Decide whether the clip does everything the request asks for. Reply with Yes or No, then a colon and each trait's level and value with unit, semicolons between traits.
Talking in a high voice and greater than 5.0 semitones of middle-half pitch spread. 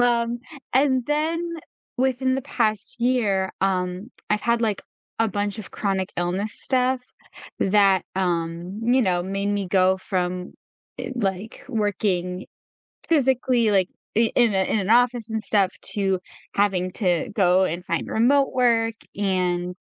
No: high, 205 Hz; average, 4.3 semitones